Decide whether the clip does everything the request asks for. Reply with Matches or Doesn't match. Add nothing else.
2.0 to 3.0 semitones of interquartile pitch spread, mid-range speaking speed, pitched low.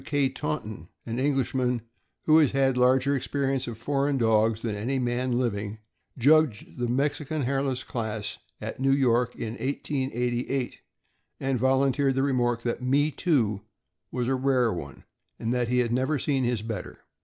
Matches